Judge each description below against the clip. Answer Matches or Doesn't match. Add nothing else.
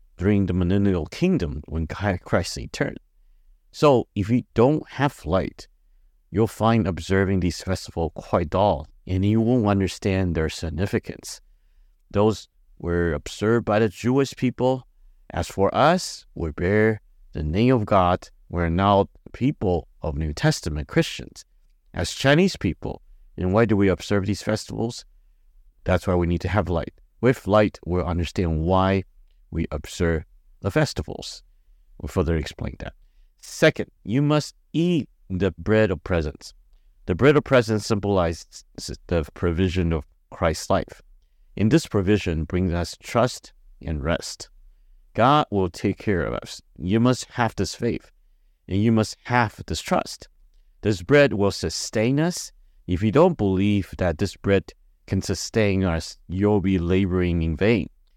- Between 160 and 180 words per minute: Doesn't match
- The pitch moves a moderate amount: Matches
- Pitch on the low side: Matches